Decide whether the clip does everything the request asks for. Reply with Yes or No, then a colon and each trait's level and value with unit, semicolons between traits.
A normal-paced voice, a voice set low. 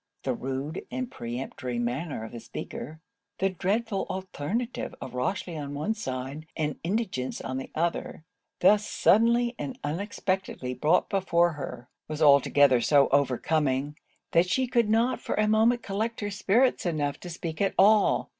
No: average, 155 wpm; medium, 165 Hz